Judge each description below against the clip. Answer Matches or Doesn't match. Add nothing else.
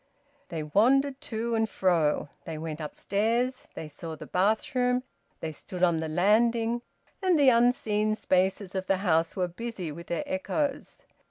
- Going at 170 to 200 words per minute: Doesn't match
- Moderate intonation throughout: Doesn't match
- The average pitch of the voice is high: Matches